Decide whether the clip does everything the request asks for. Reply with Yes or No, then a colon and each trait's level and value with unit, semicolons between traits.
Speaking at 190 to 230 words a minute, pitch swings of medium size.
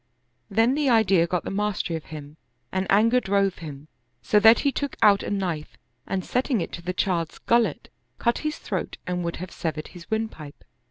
Yes: average, 195 wpm; average, 4.8 semitones